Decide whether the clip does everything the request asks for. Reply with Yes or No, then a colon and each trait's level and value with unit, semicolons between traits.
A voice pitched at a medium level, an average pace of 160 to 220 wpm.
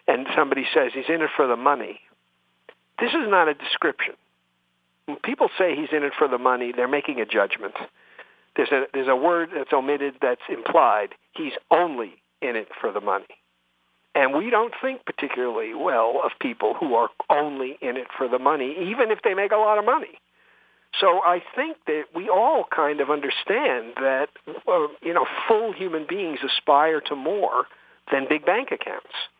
Yes: medium, 155 Hz; average, 180 wpm